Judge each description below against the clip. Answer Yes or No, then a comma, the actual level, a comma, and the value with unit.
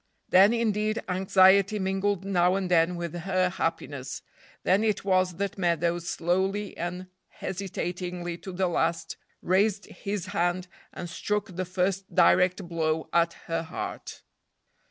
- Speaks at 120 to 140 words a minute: Yes, slow, 135 wpm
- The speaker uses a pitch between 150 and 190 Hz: Yes, medium, 185 Hz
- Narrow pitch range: Yes, narrow, 2.2 semitones